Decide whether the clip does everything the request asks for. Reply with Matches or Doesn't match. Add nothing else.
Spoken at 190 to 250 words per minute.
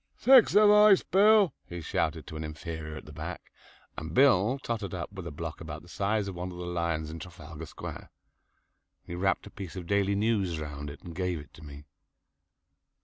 Matches